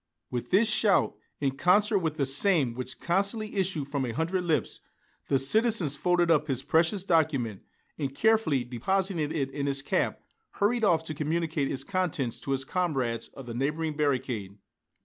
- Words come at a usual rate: Yes, average, 170 wpm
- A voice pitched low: No, medium, 155 Hz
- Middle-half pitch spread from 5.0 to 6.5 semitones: Yes, average, 5.3 semitones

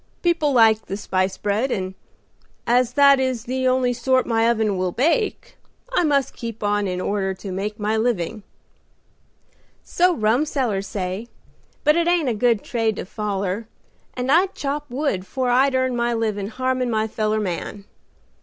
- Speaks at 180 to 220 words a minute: No, average, 165 wpm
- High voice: Yes, high, 230 Hz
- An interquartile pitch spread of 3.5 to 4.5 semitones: Yes, average, 4.0 semitones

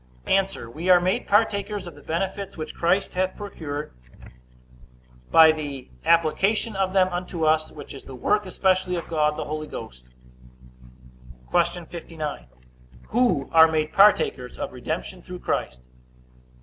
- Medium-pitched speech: Yes, medium, 170 Hz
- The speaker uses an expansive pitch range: No, average, 3.8 semitones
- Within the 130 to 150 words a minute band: Yes, average, 140 wpm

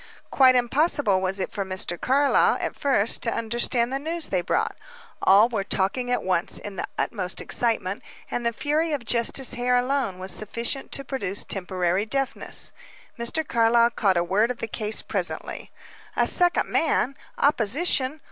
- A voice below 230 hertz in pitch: No, high, 235 Hz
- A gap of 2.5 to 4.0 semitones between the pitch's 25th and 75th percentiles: No, wide, 5.4 semitones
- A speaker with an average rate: Yes, average, 165 wpm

